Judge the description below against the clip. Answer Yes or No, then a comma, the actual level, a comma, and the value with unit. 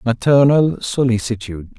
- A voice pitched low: Yes, low, 120 Hz